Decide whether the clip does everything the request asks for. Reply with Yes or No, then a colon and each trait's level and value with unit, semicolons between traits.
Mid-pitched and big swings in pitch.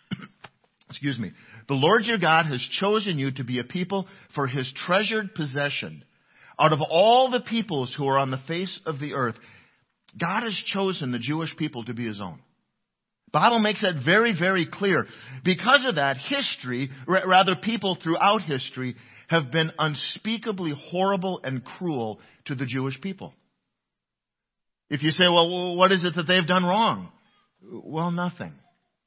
Yes: medium, 165 Hz; wide, 5.8 semitones